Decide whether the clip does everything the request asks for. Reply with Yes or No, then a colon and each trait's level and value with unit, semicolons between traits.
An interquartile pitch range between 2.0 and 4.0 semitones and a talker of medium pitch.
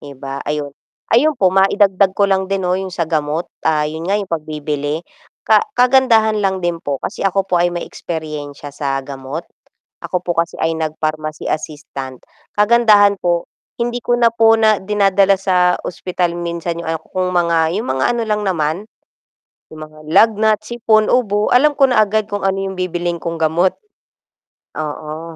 No: average, 4.7 semitones; medium, 180 Hz